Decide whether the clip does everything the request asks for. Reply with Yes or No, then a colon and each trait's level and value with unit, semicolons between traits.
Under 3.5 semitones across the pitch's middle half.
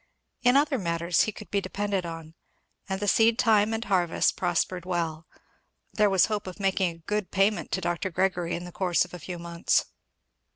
Yes: average, 3.1 semitones